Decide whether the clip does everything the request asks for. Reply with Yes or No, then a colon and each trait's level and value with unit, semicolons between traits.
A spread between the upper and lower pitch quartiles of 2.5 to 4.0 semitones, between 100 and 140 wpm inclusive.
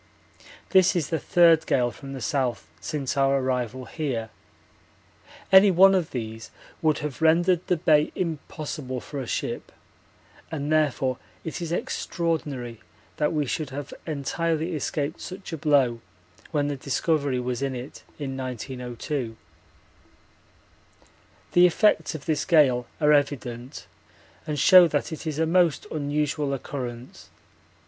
Yes: average, 3.7 semitones; slow, 135 wpm